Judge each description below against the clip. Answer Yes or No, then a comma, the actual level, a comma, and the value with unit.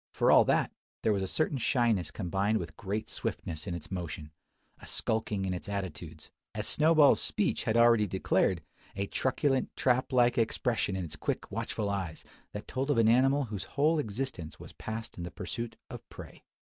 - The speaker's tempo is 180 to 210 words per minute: Yes, average, 185 wpm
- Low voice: Yes, low, 110 Hz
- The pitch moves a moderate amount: Yes, average, 4.9 semitones